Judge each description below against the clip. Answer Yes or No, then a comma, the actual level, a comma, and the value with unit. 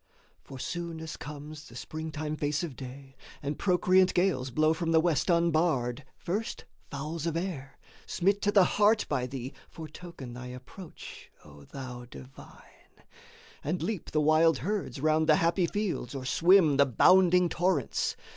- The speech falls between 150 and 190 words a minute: Yes, average, 155 wpm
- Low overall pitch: No, medium, 155 Hz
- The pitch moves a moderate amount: Yes, average, 4.4 semitones